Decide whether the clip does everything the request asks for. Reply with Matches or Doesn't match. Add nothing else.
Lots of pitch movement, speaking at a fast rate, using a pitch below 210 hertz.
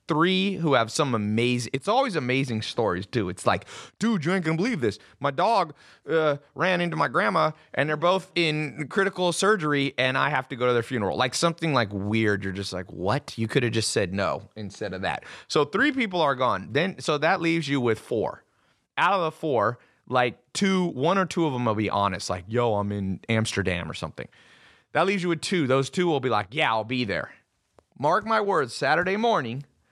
Matches